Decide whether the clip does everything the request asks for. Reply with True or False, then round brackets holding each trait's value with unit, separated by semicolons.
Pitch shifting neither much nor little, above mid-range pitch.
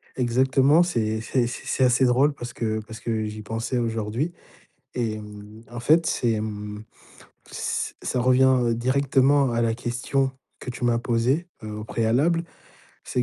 False (3.0 semitones; 120 Hz)